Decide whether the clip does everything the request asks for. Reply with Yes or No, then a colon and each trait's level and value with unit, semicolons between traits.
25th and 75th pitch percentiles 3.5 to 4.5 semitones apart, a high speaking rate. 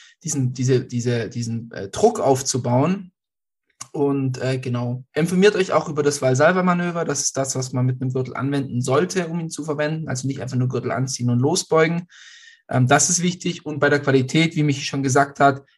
Yes: average, 3.9 semitones; fast, 195 wpm